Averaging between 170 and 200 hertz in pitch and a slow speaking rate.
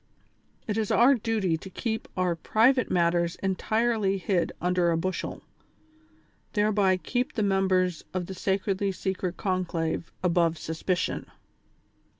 Yes: high, 190 Hz; slow, 125 wpm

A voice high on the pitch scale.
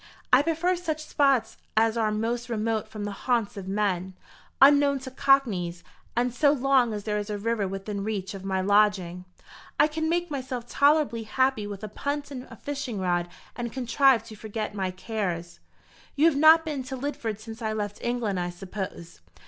Yes: high, 225 Hz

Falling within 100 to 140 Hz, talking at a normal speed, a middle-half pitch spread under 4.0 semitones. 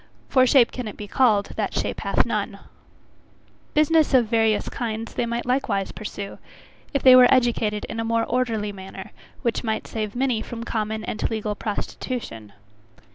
No: high, 225 Hz; average, 165 wpm; average, 2.9 semitones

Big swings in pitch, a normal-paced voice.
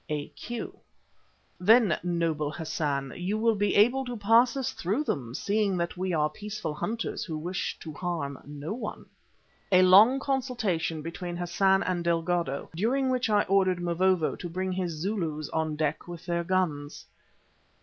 No: average, 4.6 semitones; average, 155 wpm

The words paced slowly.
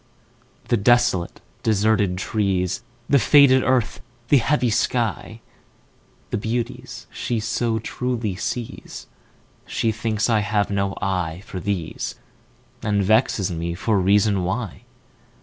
Yes: slow, 100 wpm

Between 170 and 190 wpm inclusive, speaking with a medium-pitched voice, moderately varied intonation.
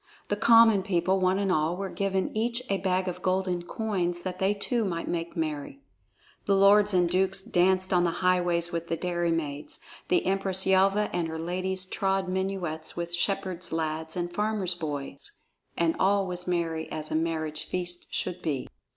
No: average, 175 wpm; medium, 180 Hz; narrow, 2.3 semitones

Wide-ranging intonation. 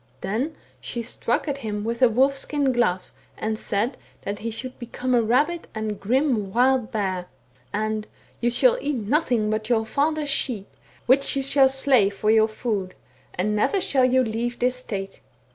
No: average, 3.7 semitones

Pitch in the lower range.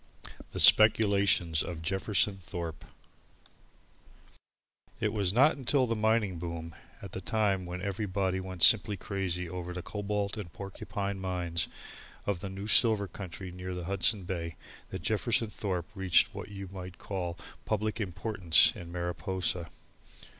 Yes: very low, 95 Hz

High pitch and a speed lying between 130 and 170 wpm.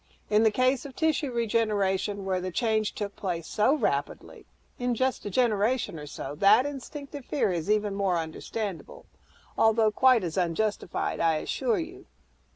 Yes: high, 215 Hz; average, 160 wpm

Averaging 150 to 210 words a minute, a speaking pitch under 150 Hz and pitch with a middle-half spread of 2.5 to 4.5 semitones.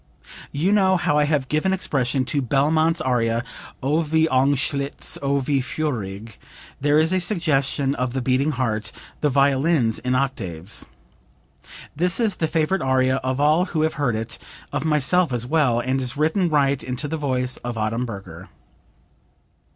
Yes: average, 160 wpm; medium, 140 Hz; average, 3.7 semitones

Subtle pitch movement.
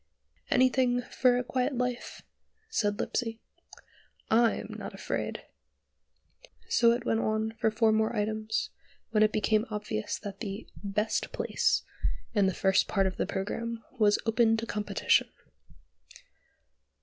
Yes: narrow, 2.1 semitones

